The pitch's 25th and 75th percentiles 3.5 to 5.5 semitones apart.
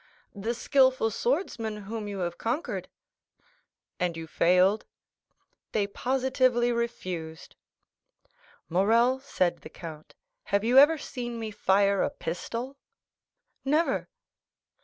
Yes: average, 5.2 semitones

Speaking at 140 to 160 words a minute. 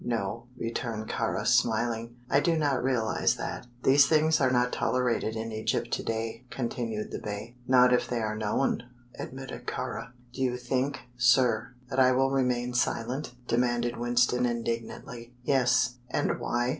Yes: average, 155 wpm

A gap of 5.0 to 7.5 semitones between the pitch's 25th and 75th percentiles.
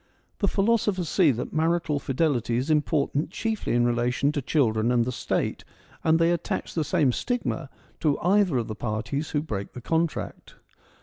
Yes: wide, 5.4 semitones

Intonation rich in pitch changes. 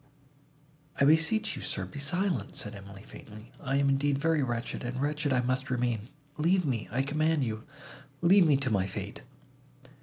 No: average, 4.4 semitones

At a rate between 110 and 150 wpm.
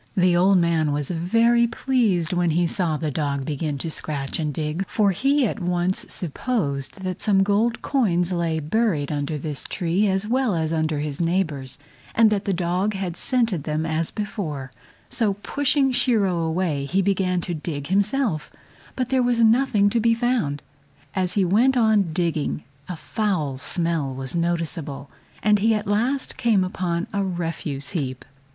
No: average, 170 wpm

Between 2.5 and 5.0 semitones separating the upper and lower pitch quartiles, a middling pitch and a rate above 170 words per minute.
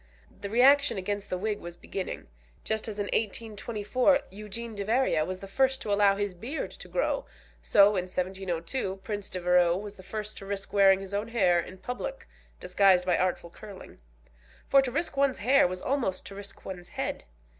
No: average, 3.6 semitones; high, 200 Hz; average, 180 wpm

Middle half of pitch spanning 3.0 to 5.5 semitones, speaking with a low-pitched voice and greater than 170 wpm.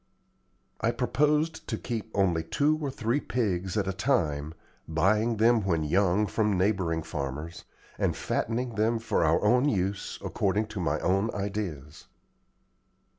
No: average, 5.0 semitones; low, 100 Hz; average, 140 wpm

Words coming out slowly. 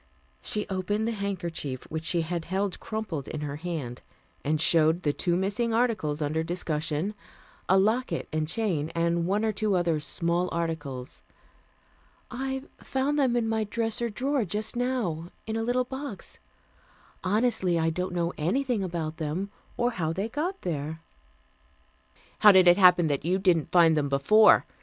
No: average, 160 wpm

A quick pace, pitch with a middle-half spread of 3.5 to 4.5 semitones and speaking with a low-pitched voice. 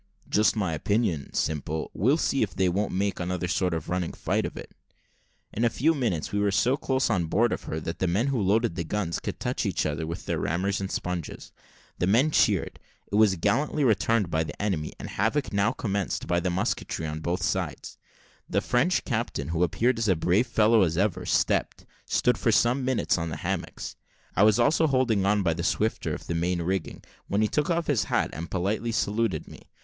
No: fast, 215 wpm; average, 5.1 semitones; low, 100 Hz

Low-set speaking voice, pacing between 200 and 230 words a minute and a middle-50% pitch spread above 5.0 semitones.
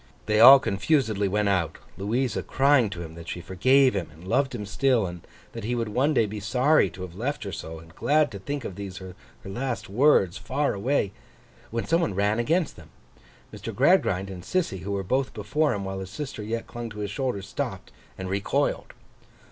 Yes: low, 105 Hz; fast, 205 wpm; wide, 5.4 semitones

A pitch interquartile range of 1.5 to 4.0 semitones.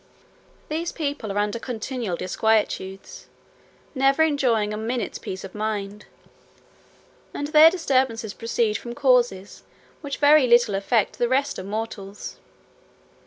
No: average, 4.7 semitones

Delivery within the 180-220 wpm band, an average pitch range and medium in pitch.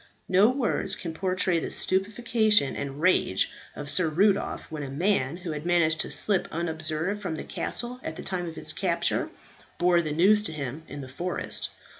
Yes: average, 185 wpm; average, 4.0 semitones; medium, 175 Hz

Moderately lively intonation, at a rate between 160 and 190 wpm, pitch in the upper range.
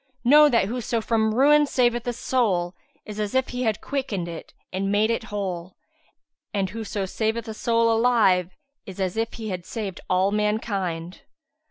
Yes: average, 3.7 semitones; average, 170 wpm; high, 215 Hz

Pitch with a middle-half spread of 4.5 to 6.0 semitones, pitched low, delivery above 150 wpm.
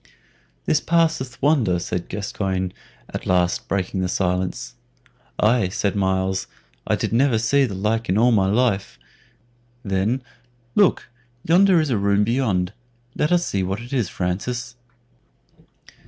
No: average, 5.2 semitones; low, 105 Hz; average, 140 wpm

